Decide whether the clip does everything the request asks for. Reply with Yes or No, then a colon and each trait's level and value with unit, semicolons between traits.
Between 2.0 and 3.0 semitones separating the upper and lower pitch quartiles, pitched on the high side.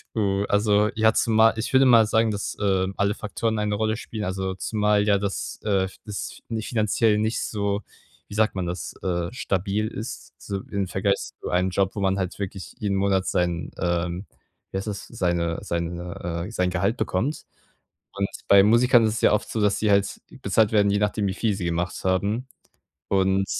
No: narrow, 2.4 semitones; low, 100 Hz